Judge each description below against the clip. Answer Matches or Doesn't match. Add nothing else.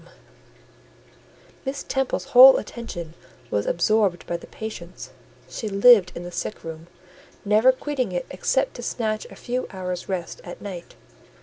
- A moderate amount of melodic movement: Doesn't match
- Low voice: Doesn't match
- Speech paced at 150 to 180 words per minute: Doesn't match